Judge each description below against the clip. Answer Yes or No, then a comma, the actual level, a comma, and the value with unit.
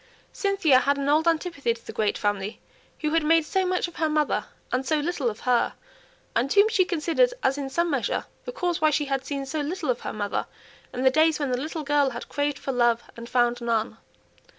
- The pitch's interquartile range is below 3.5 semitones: No, average, 4.5 semitones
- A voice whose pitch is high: Yes, very high, 285 Hz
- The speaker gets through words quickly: Yes, fast, 225 wpm